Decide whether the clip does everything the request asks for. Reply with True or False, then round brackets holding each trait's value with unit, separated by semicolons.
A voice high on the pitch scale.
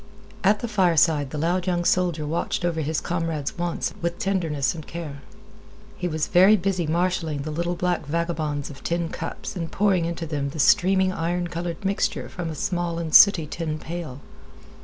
False (170 Hz)